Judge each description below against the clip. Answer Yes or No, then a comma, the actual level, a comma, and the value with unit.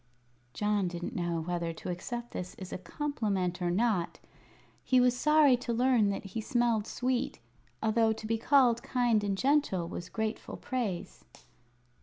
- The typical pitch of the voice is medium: No, high, 220 Hz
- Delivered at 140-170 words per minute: Yes, average, 155 wpm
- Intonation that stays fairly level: No, average, 5.1 semitones